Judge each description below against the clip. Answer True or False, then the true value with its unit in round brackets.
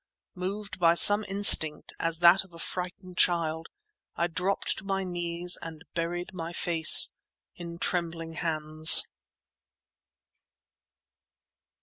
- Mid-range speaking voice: True (170 Hz)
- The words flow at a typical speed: False (110 wpm)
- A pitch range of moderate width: False (1.7 semitones)